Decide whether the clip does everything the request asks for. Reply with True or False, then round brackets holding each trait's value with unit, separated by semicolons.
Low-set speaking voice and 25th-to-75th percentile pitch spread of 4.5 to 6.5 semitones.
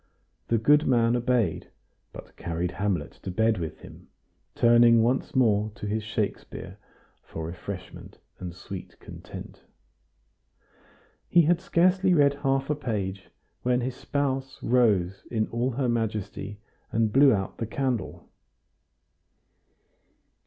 True (115 Hz; 4.8 semitones)